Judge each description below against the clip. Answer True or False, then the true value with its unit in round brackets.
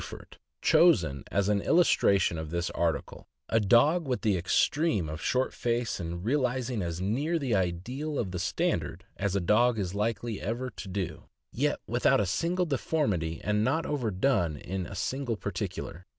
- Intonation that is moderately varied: False (6.3 semitones)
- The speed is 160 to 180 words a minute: True (170 wpm)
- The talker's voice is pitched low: True (105 Hz)